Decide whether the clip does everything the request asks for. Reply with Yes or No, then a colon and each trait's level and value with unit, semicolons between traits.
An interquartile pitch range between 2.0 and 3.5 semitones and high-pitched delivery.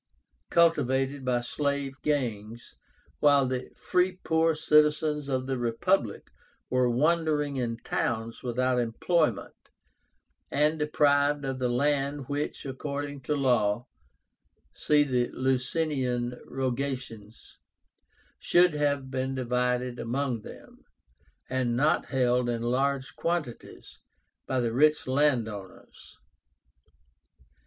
No: average, 3.1 semitones; low, 130 Hz